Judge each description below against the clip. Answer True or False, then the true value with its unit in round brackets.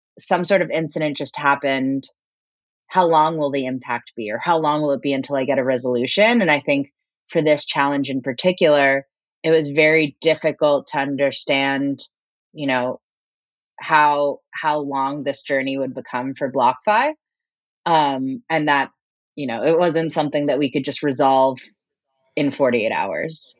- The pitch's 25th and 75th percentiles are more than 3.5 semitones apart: False (2.8 semitones)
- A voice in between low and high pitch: True (145 Hz)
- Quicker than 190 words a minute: False (165 wpm)